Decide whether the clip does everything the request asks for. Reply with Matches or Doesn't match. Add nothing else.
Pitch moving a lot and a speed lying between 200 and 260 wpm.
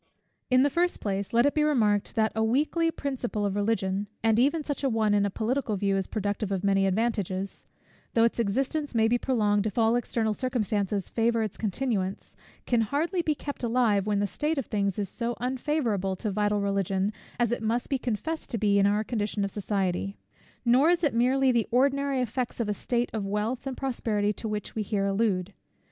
Doesn't match